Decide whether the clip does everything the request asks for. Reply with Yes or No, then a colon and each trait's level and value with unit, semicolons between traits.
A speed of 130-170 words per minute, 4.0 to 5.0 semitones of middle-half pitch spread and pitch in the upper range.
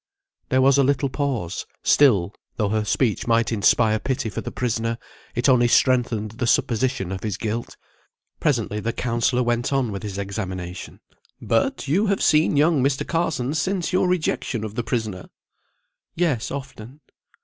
No: average, 160 wpm; average, 4.3 semitones; low, 120 Hz